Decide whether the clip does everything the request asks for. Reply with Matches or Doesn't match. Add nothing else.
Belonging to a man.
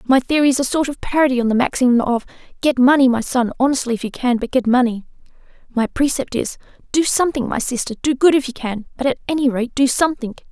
Doesn't match